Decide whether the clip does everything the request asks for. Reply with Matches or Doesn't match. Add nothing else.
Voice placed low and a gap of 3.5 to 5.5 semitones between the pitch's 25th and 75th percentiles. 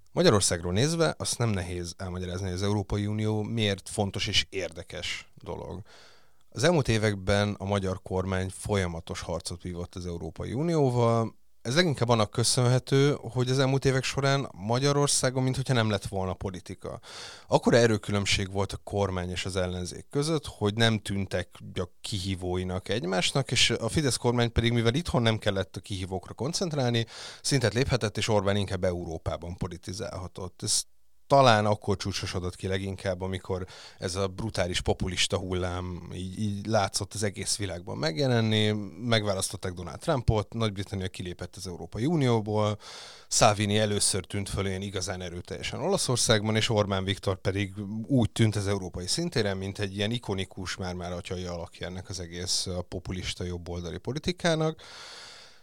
Matches